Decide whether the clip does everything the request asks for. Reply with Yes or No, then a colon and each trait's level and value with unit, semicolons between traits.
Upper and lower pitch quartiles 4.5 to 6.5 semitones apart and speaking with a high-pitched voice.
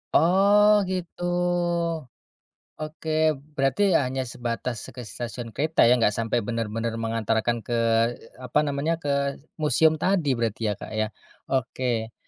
No: average, 5.0 semitones; low, 125 Hz